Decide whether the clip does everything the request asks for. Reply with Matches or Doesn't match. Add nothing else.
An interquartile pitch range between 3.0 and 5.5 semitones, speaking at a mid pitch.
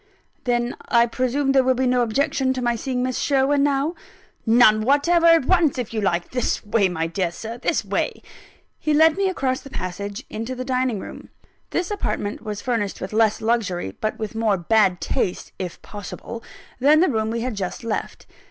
Doesn't match